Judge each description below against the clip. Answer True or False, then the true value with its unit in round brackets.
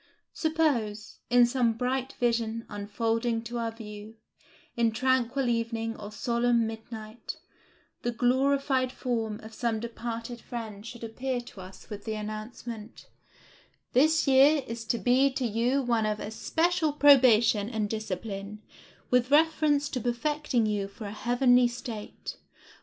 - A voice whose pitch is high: True (235 Hz)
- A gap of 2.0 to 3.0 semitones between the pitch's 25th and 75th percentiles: True (2.7 semitones)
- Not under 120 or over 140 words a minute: True (135 wpm)